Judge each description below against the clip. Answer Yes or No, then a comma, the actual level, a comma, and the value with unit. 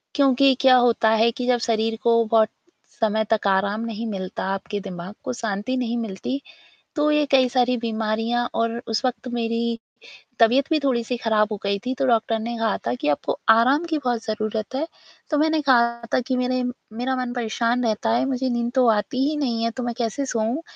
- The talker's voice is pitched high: Yes, high, 235 Hz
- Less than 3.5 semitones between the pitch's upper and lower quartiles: Yes, narrow, 2.5 semitones